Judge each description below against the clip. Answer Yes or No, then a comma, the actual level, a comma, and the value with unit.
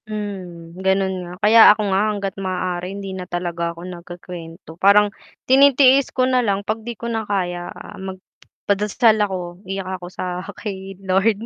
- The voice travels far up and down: No, average, 3.0 semitones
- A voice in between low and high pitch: No, high, 195 Hz